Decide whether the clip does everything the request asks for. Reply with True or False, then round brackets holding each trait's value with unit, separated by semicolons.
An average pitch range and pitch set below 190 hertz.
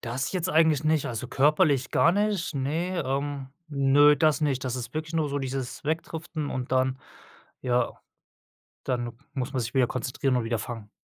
True (3.5 semitones; 135 Hz)